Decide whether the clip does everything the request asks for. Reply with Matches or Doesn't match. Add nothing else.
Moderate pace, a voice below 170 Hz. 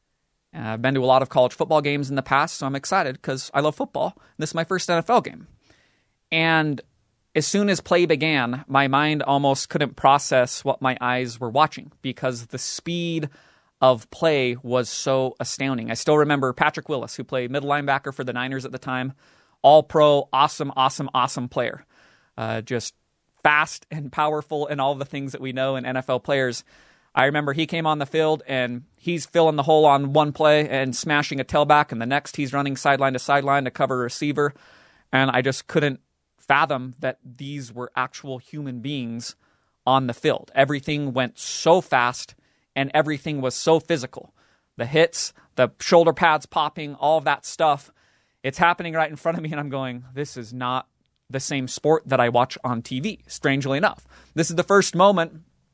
Matches